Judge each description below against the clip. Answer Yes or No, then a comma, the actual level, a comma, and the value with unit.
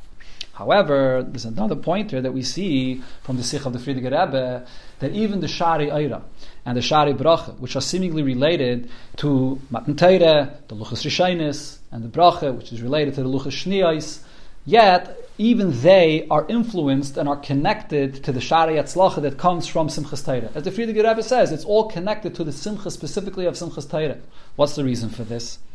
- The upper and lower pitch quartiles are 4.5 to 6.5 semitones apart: Yes, average, 4.9 semitones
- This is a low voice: No, medium, 150 Hz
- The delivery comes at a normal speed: Yes, average, 180 wpm